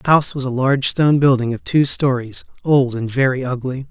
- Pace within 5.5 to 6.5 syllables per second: Yes, 5.9 syllables/s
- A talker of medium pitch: No, low, 130 Hz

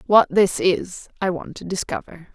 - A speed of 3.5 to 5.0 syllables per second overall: Yes, 4.5 syllables/s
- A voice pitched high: No, medium, 180 Hz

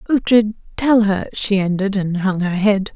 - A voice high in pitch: Yes, high, 200 Hz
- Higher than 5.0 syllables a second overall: No, 4.5 syllables/s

